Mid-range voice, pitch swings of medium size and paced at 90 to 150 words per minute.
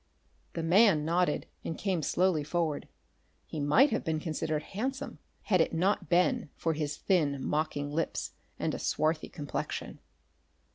Yes: medium, 165 Hz; average, 3.3 semitones; average, 145 wpm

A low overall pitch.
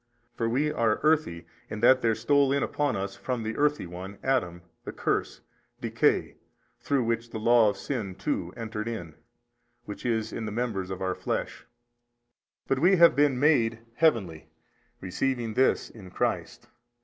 Yes: low, 115 Hz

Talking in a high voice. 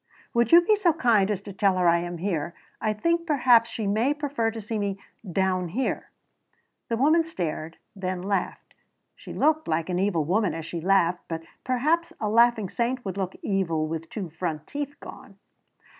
Yes: high, 200 Hz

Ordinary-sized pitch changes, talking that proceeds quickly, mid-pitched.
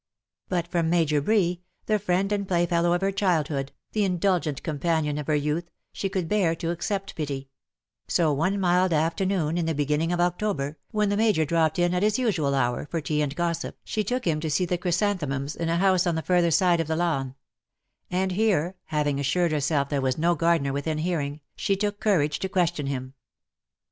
Yes: average, 3.6 semitones; fast, 210 wpm; medium, 170 Hz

